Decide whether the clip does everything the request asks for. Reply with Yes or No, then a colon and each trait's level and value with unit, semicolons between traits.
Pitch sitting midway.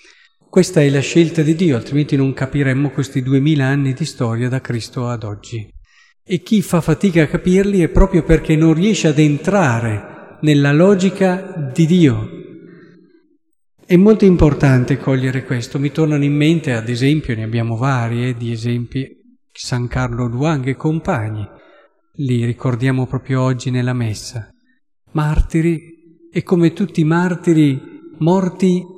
Yes: medium, 150 Hz